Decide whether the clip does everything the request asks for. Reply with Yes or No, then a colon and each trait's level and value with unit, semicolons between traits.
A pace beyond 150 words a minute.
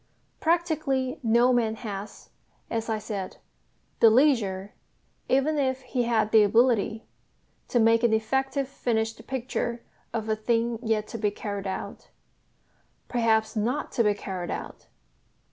No: slow, 135 wpm